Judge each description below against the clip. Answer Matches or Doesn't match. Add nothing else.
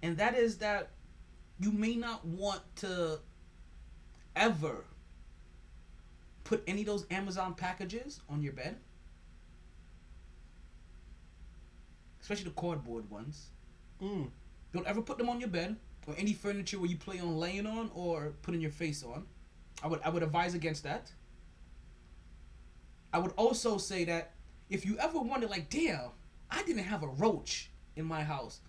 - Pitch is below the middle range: Doesn't match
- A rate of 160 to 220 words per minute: Doesn't match